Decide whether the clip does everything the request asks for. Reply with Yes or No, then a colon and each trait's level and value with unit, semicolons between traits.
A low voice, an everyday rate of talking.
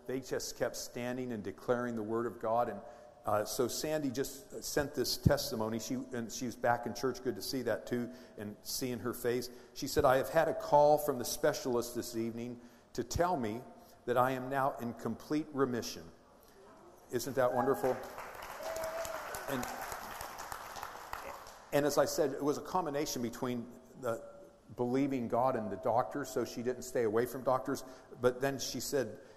Yes: low, 125 Hz; average, 175 wpm